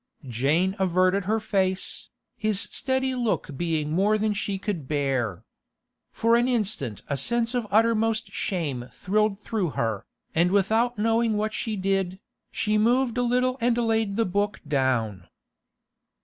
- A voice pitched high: Yes, high, 205 Hz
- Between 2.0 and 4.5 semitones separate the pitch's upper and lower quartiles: No, average, 5.3 semitones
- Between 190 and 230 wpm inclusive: No, average, 145 wpm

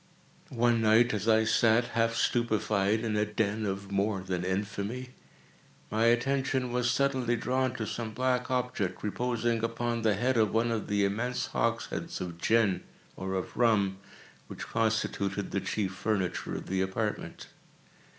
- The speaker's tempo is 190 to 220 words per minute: No, average, 150 wpm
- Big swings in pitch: No, average, 3.2 semitones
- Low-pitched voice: Yes, low, 110 Hz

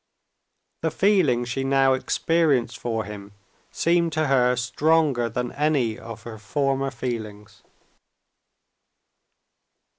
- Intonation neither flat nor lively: Yes, average, 4.3 semitones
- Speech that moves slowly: Yes, slow, 100 wpm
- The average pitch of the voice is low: Yes, low, 130 Hz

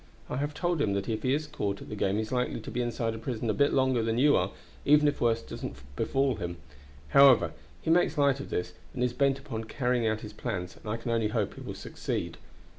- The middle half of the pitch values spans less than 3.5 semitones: No, average, 4.0 semitones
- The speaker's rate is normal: No, fast, 255 wpm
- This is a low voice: Yes, low, 120 Hz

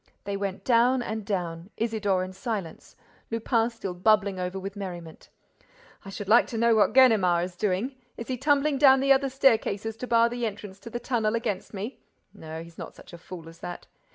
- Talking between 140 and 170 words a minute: No, average, 200 wpm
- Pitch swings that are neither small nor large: Yes, average, 4.1 semitones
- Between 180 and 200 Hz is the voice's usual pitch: No, high, 215 Hz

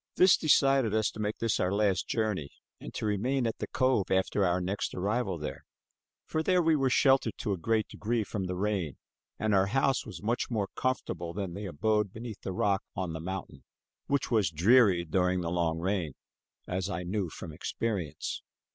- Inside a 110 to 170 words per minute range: No, average, 190 wpm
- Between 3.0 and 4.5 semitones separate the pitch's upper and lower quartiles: Yes, average, 4.2 semitones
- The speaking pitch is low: Yes, low, 100 Hz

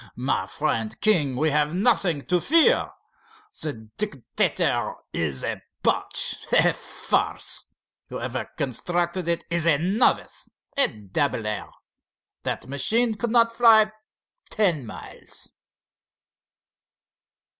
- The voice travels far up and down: Yes, wide, 8.6 semitones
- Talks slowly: Yes, slow, 100 wpm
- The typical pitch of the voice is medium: Yes, medium, 165 Hz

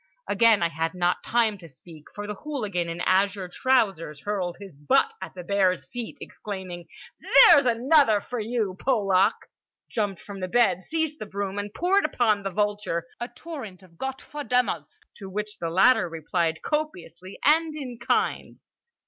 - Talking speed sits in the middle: Yes, average, 165 wpm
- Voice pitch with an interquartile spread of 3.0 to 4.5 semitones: No, average, 5.3 semitones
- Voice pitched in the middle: No, high, 205 Hz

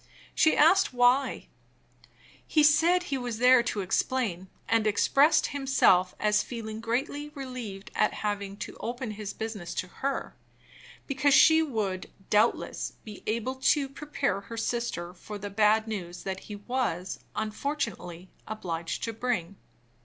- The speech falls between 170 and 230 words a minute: No, average, 140 wpm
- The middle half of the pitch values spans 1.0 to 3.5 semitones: No, average, 4.8 semitones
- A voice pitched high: Yes, high, 225 Hz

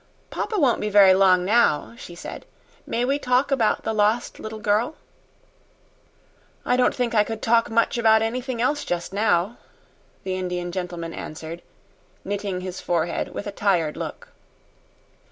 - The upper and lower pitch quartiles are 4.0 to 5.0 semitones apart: Yes, average, 4.4 semitones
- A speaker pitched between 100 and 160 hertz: No, high, 210 Hz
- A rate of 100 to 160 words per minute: Yes, average, 155 wpm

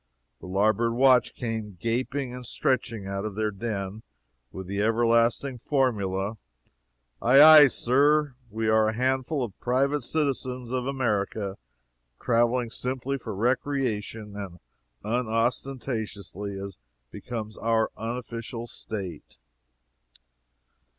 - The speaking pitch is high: No, low, 115 Hz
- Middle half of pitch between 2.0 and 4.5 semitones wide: Yes, average, 3.3 semitones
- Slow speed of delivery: Yes, slow, 110 wpm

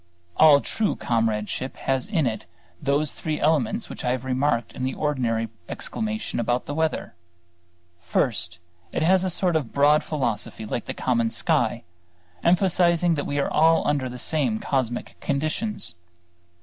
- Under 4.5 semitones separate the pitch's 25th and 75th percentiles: No, average, 4.9 semitones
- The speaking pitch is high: No, medium, 140 Hz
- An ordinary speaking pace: Yes, average, 150 wpm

